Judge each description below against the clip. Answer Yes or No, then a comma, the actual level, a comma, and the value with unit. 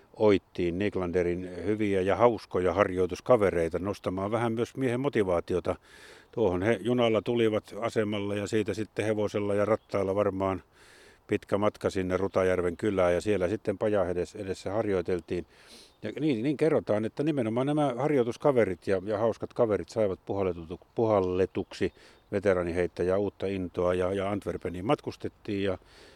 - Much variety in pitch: No, average, 3.5 semitones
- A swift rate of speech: No, average, 130 wpm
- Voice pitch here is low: Yes, low, 100 Hz